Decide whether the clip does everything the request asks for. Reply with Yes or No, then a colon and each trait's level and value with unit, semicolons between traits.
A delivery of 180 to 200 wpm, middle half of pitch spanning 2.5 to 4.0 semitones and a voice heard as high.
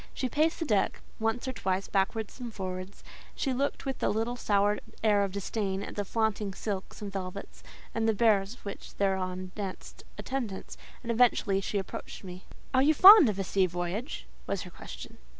Yes: average, 190 wpm; average, 3.5 semitones; high, 205 Hz